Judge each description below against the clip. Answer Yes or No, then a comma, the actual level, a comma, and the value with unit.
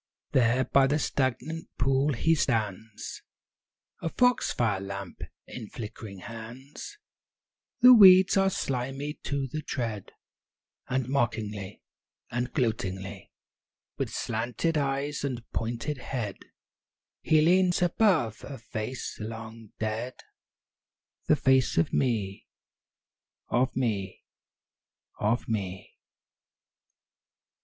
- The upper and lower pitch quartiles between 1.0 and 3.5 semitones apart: No, average, 4.4 semitones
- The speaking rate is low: Yes, slow, 100 wpm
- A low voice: Yes, low, 125 Hz